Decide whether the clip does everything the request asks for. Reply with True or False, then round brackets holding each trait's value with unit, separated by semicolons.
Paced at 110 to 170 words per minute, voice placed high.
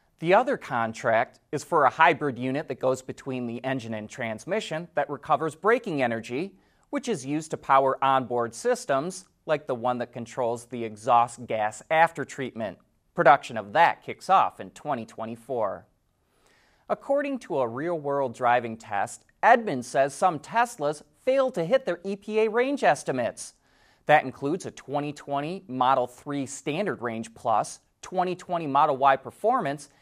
False (145 wpm; 140 Hz)